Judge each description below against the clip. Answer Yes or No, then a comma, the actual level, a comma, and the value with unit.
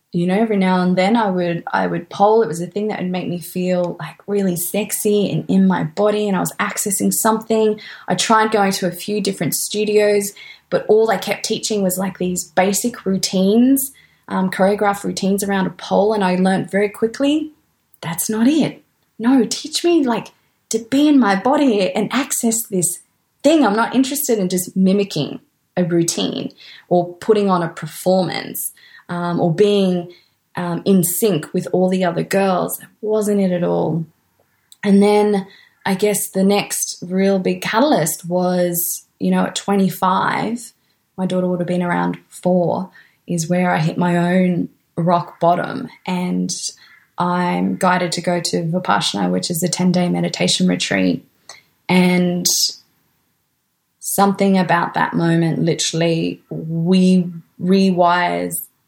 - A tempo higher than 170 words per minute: No, average, 160 wpm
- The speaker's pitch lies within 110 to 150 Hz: No, medium, 185 Hz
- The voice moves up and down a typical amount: Yes, average, 3.1 semitones